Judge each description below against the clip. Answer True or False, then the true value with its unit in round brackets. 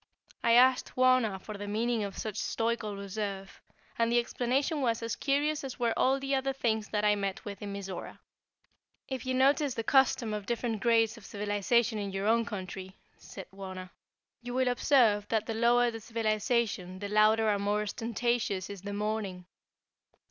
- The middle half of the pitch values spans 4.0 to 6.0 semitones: False (3.1 semitones)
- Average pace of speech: True (175 wpm)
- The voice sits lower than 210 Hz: False (220 Hz)